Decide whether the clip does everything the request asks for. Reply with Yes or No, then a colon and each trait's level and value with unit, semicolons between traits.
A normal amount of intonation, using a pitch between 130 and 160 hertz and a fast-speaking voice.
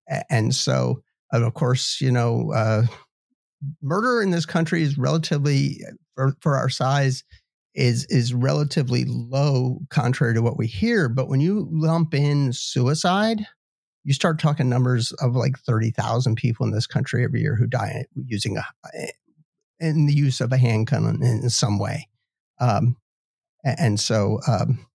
No: average, 3.8 semitones; low, 135 Hz; average, 155 wpm